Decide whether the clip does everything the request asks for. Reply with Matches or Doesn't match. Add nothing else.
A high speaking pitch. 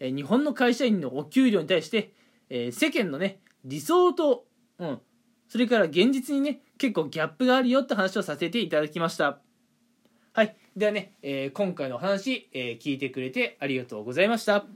Matches